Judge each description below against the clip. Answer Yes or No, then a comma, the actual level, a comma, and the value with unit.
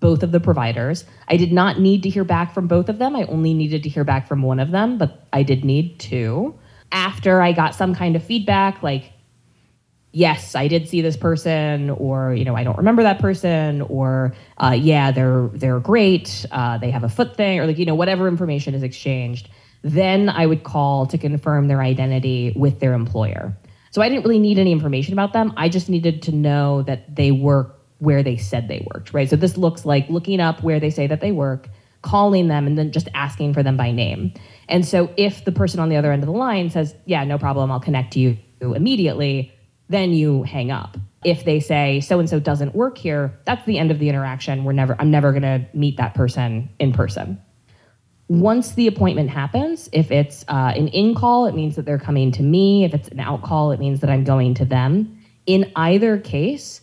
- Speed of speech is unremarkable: No, fast, 225 wpm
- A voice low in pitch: No, medium, 145 Hz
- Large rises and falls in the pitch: No, average, 5.0 semitones